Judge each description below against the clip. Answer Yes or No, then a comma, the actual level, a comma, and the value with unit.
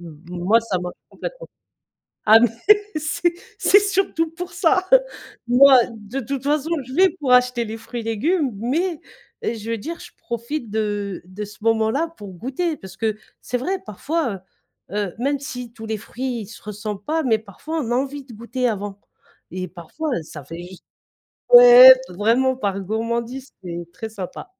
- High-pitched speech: Yes, high, 235 Hz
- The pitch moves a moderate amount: No, wide, 6.0 semitones